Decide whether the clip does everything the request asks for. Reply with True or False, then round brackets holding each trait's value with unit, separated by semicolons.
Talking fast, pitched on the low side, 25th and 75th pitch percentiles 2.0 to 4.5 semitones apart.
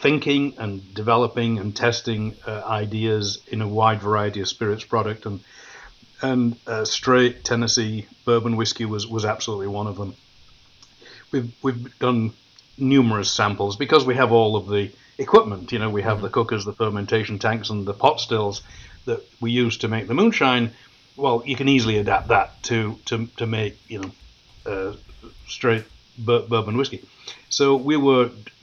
False (165 wpm; 110 Hz; 2.7 semitones)